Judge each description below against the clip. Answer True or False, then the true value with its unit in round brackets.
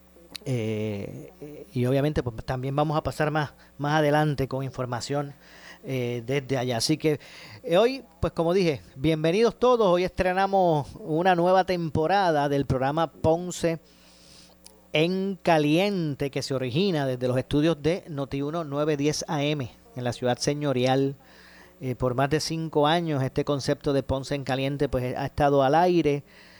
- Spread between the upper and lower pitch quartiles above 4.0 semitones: False (3.6 semitones)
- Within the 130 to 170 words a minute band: True (145 wpm)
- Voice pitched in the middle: True (145 Hz)